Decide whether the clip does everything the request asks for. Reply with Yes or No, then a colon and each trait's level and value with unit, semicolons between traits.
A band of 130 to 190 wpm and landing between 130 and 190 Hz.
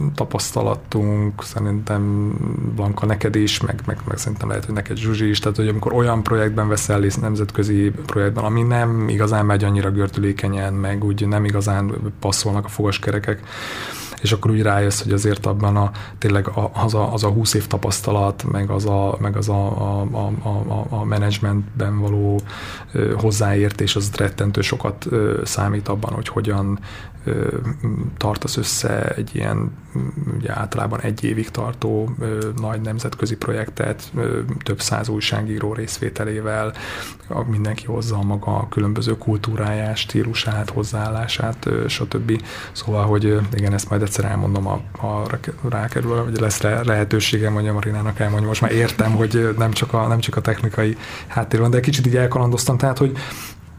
No: average, 150 wpm; low, 105 Hz